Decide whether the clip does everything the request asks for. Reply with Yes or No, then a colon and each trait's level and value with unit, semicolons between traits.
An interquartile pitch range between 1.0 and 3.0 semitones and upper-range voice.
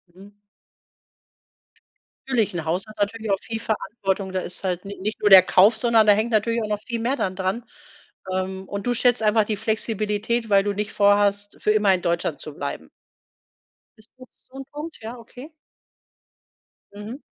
Yes: narrow, 2.5 semitones; high, 210 Hz